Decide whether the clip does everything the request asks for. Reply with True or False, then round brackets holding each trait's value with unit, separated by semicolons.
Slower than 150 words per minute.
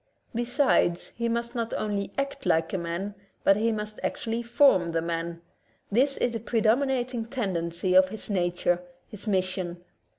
False (160 wpm)